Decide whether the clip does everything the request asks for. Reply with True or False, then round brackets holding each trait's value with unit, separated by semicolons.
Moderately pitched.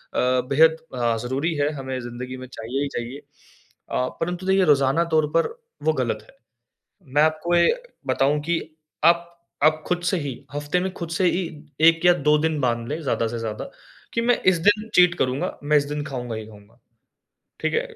True (145 Hz)